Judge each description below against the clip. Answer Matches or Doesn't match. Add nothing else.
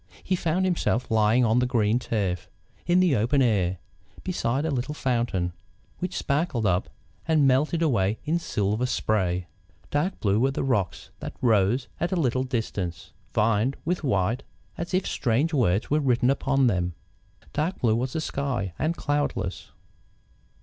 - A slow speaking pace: Doesn't match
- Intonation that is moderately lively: Doesn't match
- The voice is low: Matches